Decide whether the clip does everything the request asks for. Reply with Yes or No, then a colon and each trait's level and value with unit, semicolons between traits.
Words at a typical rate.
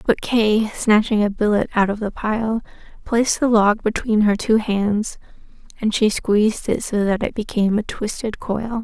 Yes: average, 185 wpm